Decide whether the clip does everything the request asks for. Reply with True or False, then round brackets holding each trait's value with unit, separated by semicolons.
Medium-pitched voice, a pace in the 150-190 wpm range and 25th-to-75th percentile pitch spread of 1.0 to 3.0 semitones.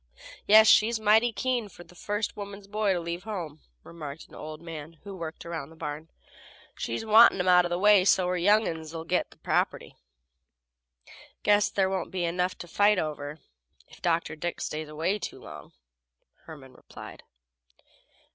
False (180 Hz; 170 wpm; 4.3 semitones)